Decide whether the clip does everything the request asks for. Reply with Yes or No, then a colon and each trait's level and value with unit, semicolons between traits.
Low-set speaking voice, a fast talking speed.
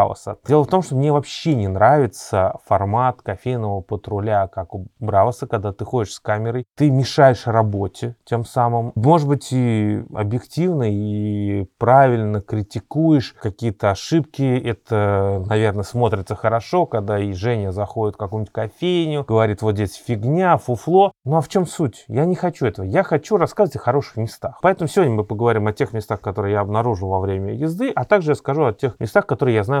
Yes: low, 115 Hz; fast, 175 wpm